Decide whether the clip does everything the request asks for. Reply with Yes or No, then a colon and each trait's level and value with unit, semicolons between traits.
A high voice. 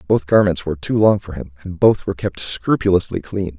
No: very low, 95 Hz